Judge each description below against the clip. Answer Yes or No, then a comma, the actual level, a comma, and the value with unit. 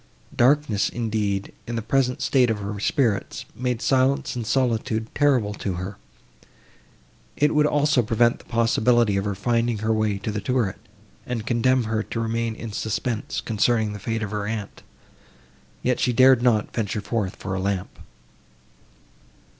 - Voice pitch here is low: Yes, low, 115 Hz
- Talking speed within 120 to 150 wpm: No, average, 160 wpm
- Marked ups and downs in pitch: No, average, 2.9 semitones